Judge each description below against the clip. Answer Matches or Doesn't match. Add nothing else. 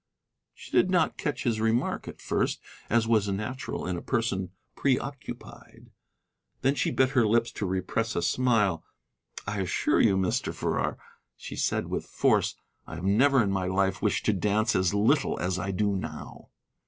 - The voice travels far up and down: Doesn't match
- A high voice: Doesn't match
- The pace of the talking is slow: Doesn't match